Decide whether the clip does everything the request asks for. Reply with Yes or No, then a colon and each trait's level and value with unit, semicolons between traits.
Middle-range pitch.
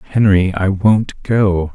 No: low, 100 Hz